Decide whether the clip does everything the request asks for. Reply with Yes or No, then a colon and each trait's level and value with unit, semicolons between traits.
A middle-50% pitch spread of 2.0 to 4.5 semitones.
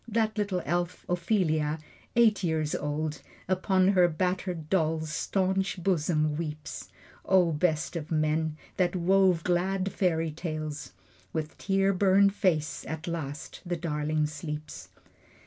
Yes: average, 3.4 semitones